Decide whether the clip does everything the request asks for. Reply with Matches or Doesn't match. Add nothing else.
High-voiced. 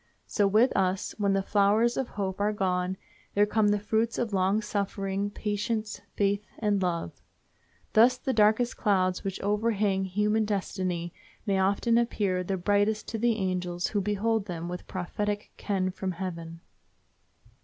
Matches